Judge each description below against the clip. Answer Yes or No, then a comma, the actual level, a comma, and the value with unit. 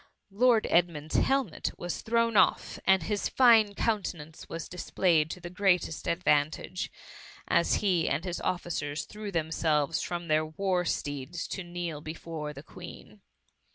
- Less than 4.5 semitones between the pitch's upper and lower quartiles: Yes, average, 3.8 semitones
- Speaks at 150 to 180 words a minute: No, average, 140 wpm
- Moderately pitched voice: Yes, medium, 175 Hz